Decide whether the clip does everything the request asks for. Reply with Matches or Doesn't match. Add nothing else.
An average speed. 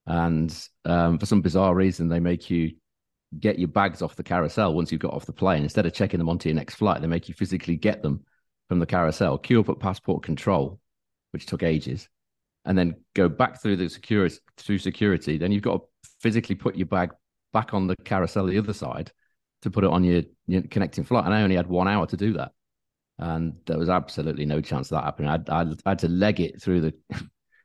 Doesn't match